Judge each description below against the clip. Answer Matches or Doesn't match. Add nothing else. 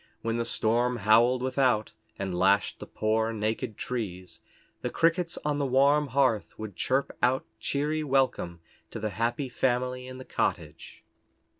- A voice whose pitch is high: Doesn't match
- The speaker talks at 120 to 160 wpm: Matches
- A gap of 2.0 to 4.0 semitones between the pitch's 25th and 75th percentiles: Matches